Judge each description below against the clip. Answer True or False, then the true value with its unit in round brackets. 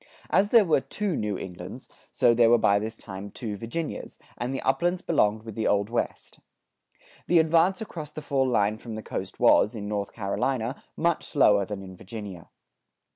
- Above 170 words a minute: True (180 wpm)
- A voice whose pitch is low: True (115 Hz)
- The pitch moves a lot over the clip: True (6.8 semitones)